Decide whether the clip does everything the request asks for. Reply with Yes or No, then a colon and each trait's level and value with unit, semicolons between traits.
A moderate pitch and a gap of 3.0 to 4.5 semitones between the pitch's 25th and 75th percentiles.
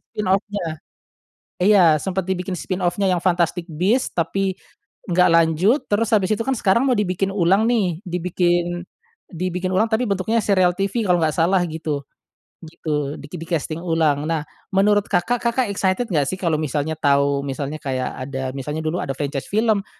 Yes: medium, 180 Hz; average, 3.9 semitones